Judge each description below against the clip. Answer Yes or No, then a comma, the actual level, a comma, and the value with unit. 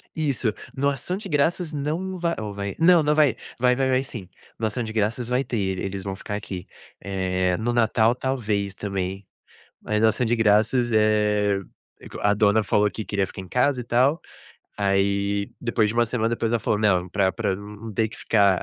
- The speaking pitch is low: Yes, low, 110 Hz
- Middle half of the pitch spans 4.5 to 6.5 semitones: No, average, 3.7 semitones